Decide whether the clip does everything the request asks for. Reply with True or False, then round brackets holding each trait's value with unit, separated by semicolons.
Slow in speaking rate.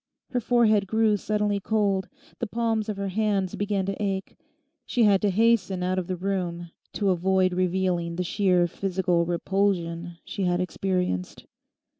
False (155 wpm)